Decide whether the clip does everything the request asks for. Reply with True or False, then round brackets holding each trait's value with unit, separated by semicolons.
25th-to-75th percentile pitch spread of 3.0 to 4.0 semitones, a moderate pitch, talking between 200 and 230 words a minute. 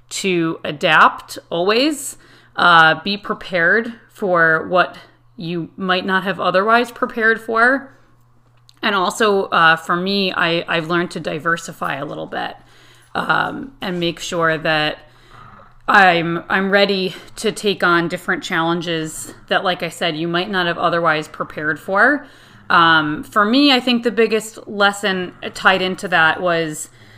False (3.7 semitones; 180 Hz; 140 wpm)